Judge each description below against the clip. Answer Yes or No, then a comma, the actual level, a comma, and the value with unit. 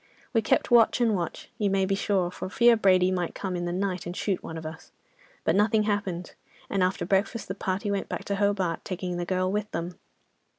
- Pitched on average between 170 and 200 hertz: Yes, high, 190 Hz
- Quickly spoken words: Yes, fast, 220 wpm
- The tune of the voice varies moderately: No, narrow, 2.3 semitones